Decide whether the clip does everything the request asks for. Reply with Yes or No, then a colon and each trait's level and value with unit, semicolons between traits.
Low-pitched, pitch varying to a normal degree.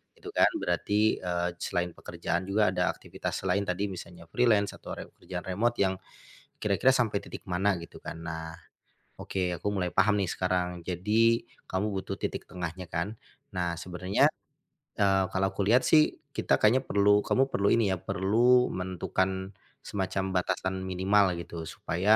No: very low, 95 Hz; narrow, 2.3 semitones